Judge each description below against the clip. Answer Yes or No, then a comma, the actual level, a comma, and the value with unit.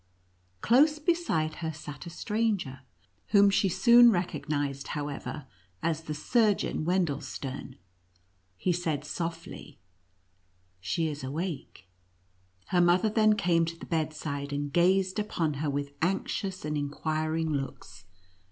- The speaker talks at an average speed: No, slow, 125 wpm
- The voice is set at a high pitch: No, medium, 160 Hz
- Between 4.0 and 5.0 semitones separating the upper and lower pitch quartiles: Yes, average, 4.7 semitones